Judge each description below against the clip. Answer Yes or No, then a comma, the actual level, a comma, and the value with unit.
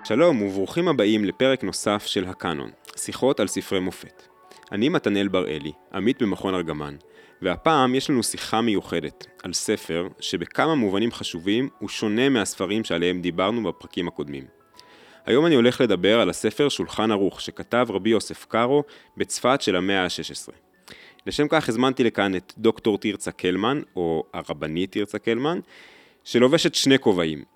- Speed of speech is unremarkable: Yes, average, 140 wpm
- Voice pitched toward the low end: Yes, low, 100 Hz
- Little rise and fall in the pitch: No, wide, 5.6 semitones